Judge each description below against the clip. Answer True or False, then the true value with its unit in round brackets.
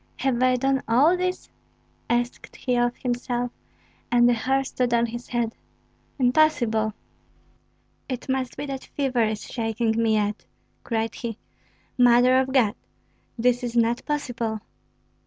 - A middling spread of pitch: False (2.2 semitones)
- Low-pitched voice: False (245 Hz)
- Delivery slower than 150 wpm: True (140 wpm)